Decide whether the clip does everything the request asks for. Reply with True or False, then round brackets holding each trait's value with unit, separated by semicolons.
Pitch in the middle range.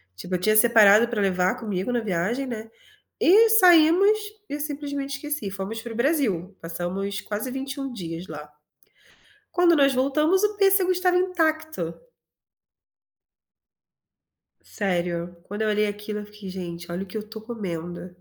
False (220 Hz)